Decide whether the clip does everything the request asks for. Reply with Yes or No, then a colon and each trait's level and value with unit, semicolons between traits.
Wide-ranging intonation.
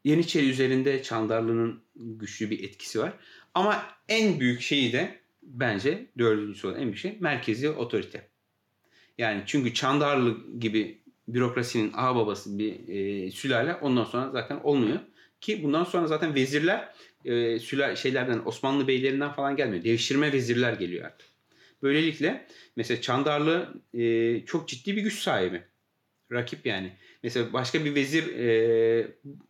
No: average, 4.5 semitones